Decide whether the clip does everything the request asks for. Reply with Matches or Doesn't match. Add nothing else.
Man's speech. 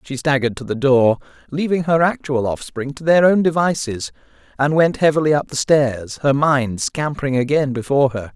Matches